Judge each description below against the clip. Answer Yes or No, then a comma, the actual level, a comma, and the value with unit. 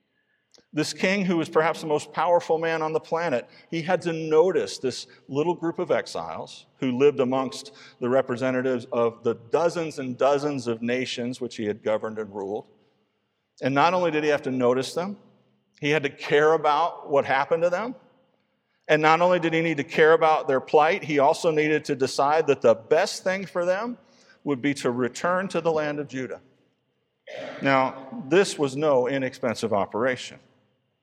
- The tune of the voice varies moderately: Yes, average, 4.5 semitones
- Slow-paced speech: No, average, 180 wpm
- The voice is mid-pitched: Yes, medium, 150 Hz